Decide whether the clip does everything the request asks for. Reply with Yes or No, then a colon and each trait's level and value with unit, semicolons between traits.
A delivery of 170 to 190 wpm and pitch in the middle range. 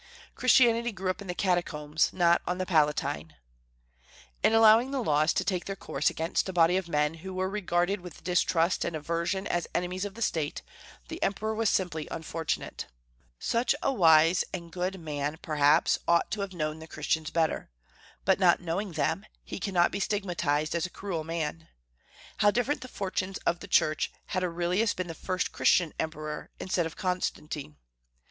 Yes: average, 175 wpm; medium, 175 Hz